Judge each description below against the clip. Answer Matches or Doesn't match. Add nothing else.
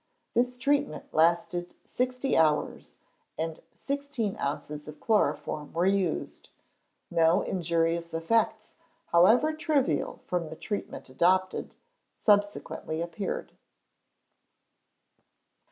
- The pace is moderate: Doesn't match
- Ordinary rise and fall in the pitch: Doesn't match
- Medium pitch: Matches